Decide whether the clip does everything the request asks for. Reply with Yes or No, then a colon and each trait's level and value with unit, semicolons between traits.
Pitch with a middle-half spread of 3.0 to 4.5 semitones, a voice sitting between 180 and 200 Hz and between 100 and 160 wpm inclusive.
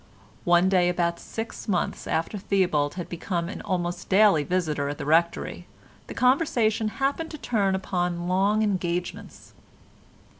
Yes: average, 3.4 semitones; medium, 185 Hz; average, 140 wpm